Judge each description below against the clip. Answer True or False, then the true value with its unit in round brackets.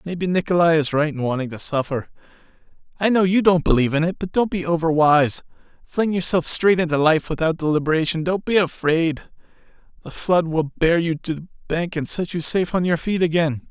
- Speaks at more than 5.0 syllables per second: True (5.7 syllables/s)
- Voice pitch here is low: False (165 Hz)